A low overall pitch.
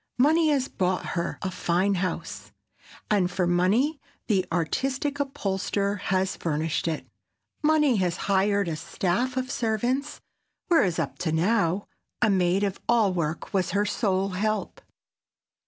No: high, 195 Hz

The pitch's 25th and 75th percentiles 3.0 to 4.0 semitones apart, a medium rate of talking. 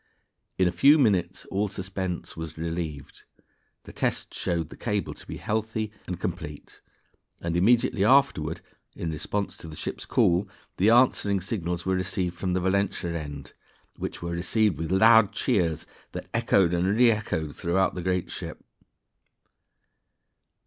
Yes: average, 3.4 semitones; average, 145 wpm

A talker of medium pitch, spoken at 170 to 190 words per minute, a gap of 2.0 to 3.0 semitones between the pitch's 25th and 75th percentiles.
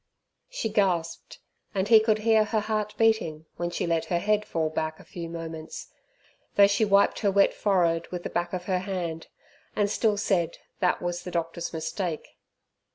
No: medium, 180 Hz; average, 180 wpm; average, 3.8 semitones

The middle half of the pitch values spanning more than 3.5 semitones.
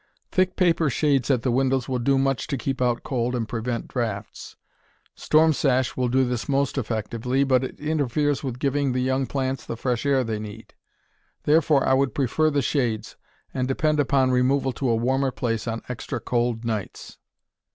No: narrow, 2.6 semitones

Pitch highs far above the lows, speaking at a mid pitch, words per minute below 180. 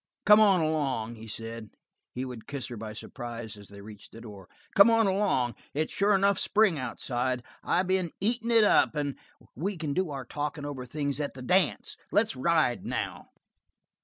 No: wide, 7.9 semitones; medium, 145 Hz; average, 185 wpm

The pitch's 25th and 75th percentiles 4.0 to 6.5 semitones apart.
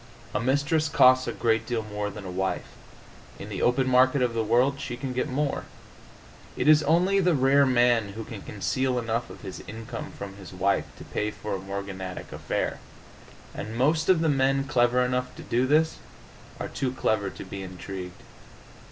Yes: average, 4.6 semitones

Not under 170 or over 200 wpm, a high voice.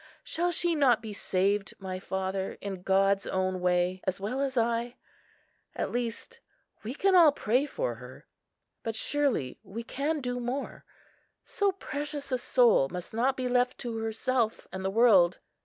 No: average, 155 wpm; high, 235 Hz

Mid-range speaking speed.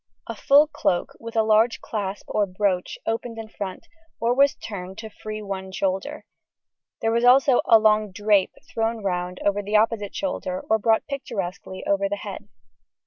Yes: average, 170 wpm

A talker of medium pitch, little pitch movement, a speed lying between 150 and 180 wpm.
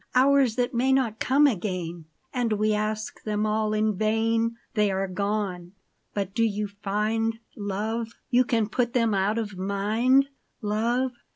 No: high, 215 Hz; narrow, 2.3 semitones; average, 155 wpm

